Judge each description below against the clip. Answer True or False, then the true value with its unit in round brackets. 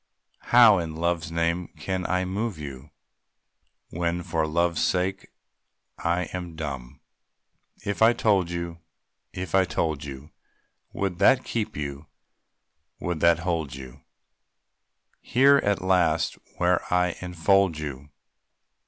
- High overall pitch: False (85 Hz)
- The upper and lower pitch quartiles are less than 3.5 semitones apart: True (2.9 semitones)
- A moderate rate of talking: False (120 wpm)